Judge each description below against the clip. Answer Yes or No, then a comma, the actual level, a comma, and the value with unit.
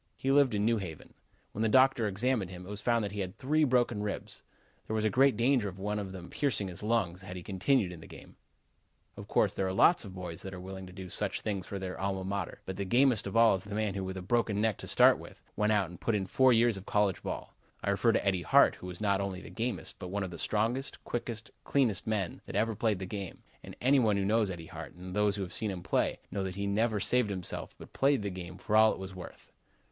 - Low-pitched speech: Yes, low, 100 Hz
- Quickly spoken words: Yes, fast, 265 wpm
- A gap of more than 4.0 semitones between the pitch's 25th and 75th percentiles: No, average, 3.2 semitones